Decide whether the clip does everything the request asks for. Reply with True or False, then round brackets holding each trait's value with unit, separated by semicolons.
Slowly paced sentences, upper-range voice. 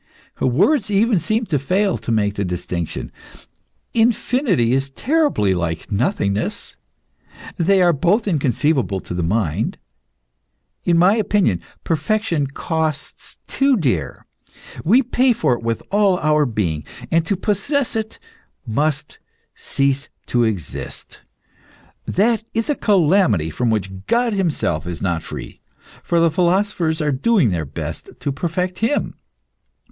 False (130 wpm; 160 Hz)